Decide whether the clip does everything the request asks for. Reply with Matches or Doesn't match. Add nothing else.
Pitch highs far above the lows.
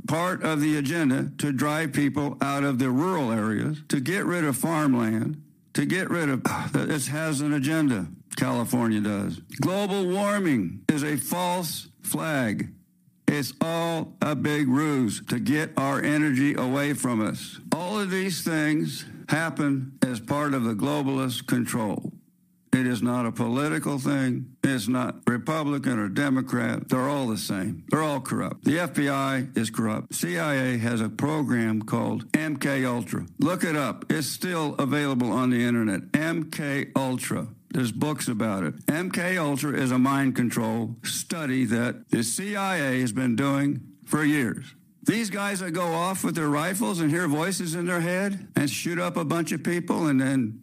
Doesn't match